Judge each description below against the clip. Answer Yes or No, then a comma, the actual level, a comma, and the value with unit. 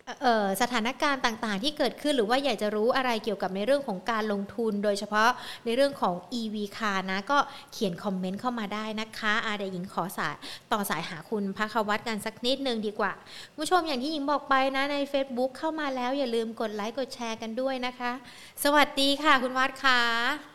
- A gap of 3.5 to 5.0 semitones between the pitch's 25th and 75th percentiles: Yes, average, 4.2 semitones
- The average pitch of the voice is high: Yes, high, 235 Hz